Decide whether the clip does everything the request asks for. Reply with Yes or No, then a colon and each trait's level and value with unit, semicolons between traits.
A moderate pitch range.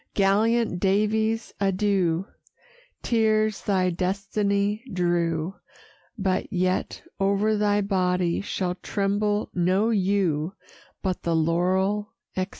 No: narrow, 2.3 semitones